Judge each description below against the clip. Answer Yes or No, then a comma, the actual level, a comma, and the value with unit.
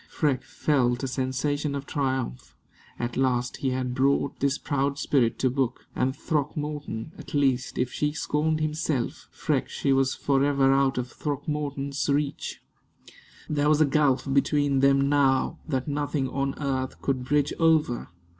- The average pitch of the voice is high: No, medium, 140 Hz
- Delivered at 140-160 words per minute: Yes, average, 150 wpm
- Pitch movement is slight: Yes, narrow, 2.0 semitones